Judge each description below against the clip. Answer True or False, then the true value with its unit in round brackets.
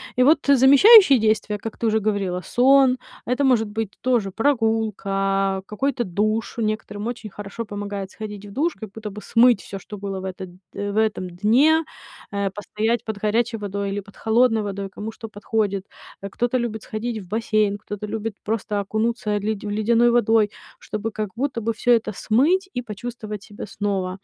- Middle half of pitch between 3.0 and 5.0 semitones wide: False (2.5 semitones)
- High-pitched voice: True (215 Hz)